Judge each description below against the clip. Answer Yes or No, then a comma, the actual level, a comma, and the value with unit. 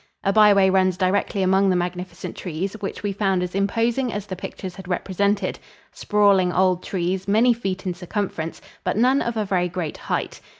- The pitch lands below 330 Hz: Yes, high, 190 Hz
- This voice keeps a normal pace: Yes, average, 175 wpm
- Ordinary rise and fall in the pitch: No, narrow, 2.0 semitones